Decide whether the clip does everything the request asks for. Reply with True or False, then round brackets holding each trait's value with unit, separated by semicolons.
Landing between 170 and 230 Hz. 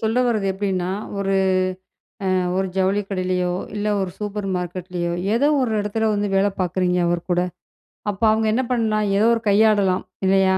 True (195 Hz)